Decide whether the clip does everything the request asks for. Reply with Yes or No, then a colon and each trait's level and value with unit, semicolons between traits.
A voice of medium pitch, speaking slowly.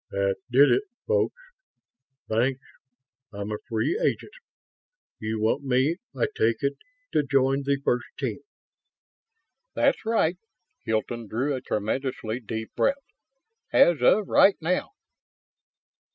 No: low, 130 Hz; slow, 120 wpm